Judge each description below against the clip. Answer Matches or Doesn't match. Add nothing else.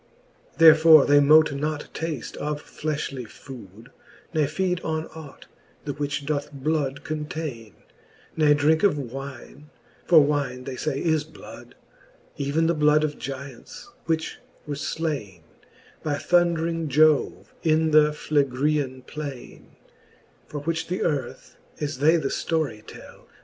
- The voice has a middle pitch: Matches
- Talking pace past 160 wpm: Doesn't match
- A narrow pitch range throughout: Matches